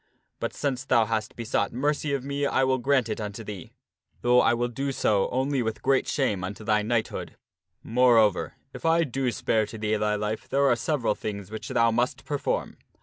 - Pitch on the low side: Yes, low, 120 Hz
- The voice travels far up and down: No, average, 3.8 semitones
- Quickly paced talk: Yes, fast, 220 wpm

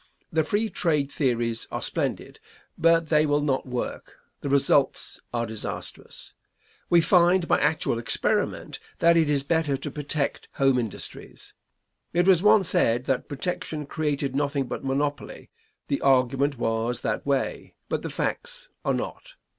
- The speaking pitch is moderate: Yes, medium, 145 Hz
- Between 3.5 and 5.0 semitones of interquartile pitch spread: Yes, average, 3.9 semitones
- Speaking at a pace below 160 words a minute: Yes, average, 145 wpm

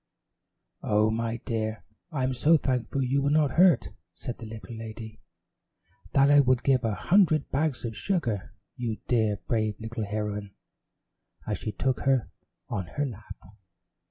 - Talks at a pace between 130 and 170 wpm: Yes, average, 150 wpm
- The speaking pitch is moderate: No, low, 120 Hz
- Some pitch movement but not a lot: Yes, average, 4.0 semitones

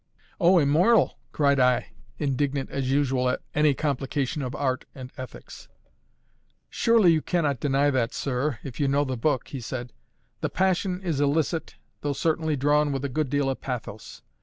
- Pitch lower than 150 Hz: Yes, medium, 140 Hz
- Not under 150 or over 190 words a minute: Yes, average, 165 wpm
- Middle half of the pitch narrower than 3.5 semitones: Yes, average, 2.8 semitones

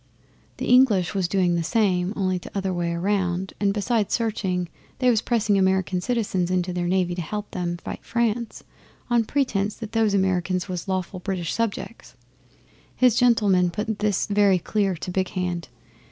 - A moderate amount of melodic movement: Yes, average, 3.0 semitones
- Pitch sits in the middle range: No, high, 195 Hz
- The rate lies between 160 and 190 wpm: Yes, average, 165 wpm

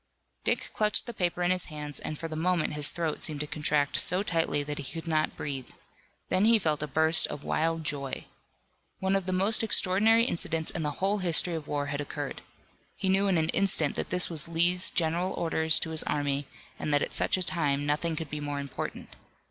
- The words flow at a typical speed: No, fast, 215 wpm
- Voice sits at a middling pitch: Yes, medium, 160 Hz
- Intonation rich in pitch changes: No, average, 3.6 semitones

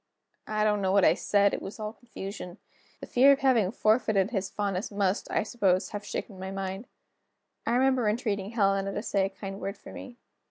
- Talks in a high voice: Yes, high, 205 Hz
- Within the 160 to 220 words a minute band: Yes, average, 200 wpm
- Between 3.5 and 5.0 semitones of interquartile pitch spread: No, narrow, 2.4 semitones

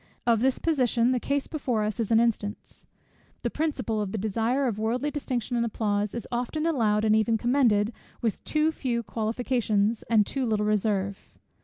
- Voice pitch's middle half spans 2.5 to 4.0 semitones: Yes, average, 3.1 semitones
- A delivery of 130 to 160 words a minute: No, average, 175 wpm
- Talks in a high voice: Yes, high, 230 Hz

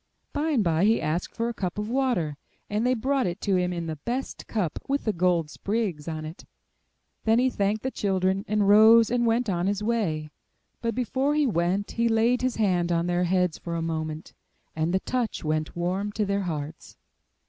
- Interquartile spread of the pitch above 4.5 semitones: Yes, average, 5.2 semitones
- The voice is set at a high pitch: Yes, high, 200 Hz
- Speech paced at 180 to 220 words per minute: Yes, fast, 205 wpm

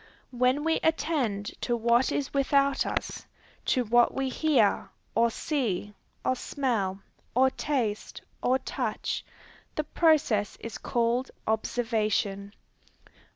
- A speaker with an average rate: No, slow, 110 wpm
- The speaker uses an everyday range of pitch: Yes, average, 4.1 semitones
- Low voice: No, high, 245 Hz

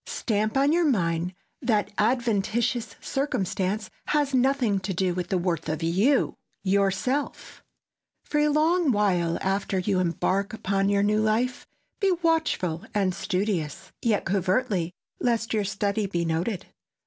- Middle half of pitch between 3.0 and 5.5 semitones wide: Yes, average, 4.8 semitones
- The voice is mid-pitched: No, high, 205 Hz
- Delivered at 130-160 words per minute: Yes, slow, 135 wpm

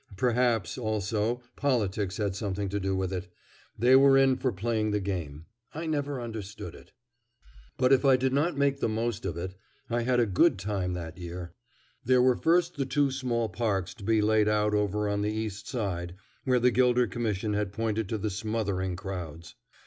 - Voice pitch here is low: Yes, low, 110 Hz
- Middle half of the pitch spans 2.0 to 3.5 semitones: No, average, 4.4 semitones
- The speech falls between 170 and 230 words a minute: Yes, average, 190 wpm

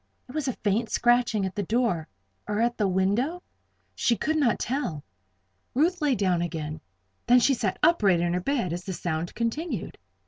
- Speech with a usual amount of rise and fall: No, wide, 6.1 semitones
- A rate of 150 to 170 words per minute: No, average, 180 wpm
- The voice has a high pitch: Yes, high, 220 Hz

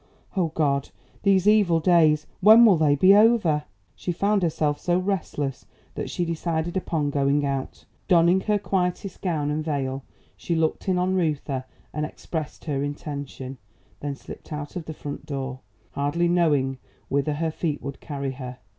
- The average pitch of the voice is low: No, medium, 155 Hz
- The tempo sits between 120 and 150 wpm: No, average, 165 wpm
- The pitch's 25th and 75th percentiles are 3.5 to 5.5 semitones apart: Yes, average, 3.8 semitones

